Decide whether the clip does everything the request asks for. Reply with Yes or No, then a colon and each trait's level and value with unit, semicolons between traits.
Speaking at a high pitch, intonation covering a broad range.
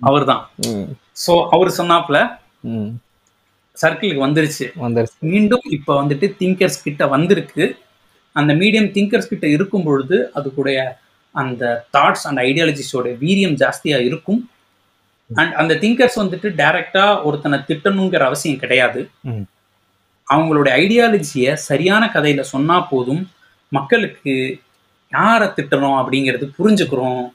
No: medium, 150 Hz; wide, 6.6 semitones